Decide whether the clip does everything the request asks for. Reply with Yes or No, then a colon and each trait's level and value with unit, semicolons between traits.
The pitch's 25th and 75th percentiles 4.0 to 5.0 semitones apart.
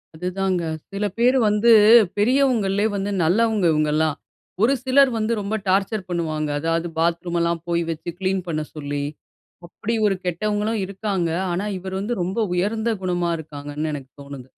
Yes: average, 4.3 semitones